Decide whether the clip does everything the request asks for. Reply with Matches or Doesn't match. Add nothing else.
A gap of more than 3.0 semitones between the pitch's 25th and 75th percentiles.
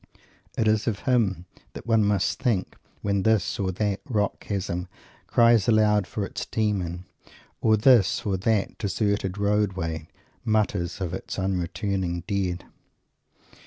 Doesn't match